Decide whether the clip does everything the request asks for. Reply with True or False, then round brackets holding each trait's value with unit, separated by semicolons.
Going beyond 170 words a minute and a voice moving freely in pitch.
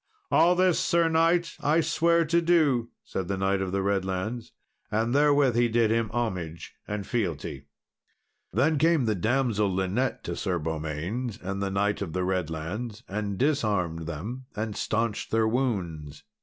False (155 wpm; 5.8 semitones)